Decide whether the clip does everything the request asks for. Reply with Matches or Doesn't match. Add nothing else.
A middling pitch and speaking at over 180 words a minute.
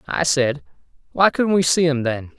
Matches